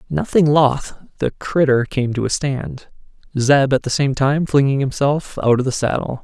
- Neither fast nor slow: Yes, average, 185 wpm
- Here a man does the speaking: Yes, male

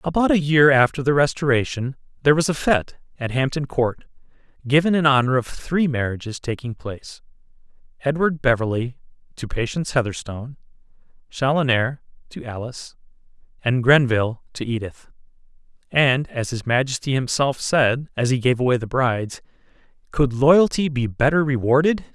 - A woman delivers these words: No, male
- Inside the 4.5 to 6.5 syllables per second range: Yes, 5.3 syllables/s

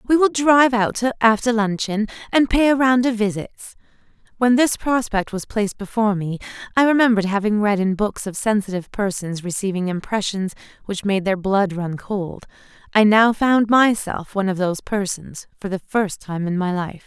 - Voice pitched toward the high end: Yes, high, 210 Hz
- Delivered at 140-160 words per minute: No, average, 180 wpm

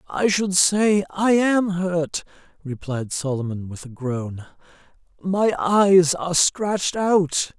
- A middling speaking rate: No, slow, 125 wpm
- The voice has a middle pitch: Yes, medium, 170 Hz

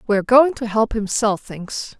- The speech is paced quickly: Yes, fast, 210 wpm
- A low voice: No, high, 220 Hz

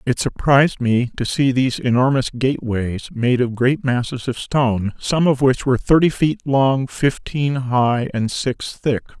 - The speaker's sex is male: Yes, male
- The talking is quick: No, average, 175 wpm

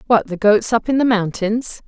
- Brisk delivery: Yes, fast, 225 wpm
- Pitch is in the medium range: No, high, 220 Hz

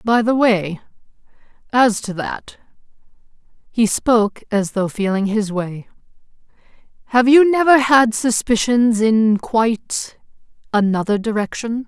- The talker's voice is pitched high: Yes, high, 225 Hz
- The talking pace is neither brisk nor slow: No, slow, 100 wpm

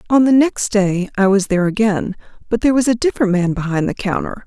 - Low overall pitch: No, high, 210 Hz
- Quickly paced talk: Yes, fast, 230 wpm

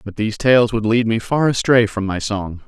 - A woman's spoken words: No, male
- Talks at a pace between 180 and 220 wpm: No, fast, 245 wpm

